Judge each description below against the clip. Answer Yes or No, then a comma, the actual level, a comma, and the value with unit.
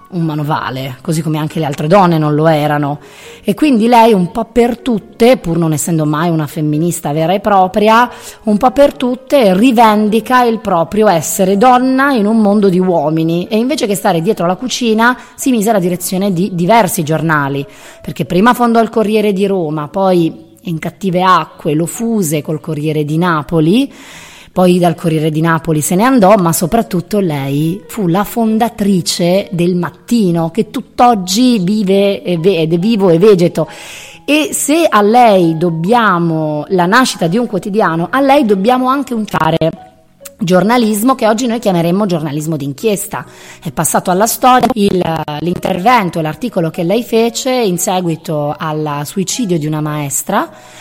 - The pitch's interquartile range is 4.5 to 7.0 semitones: Yes, wide, 5.6 semitones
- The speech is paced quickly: No, average, 160 wpm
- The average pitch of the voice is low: No, high, 190 Hz